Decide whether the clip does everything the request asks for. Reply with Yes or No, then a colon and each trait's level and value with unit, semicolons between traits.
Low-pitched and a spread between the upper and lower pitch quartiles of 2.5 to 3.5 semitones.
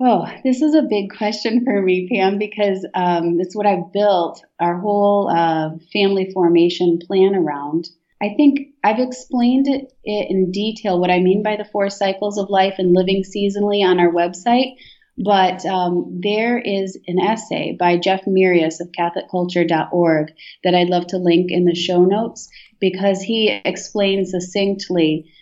No: high, 190 Hz; average, 2.8 semitones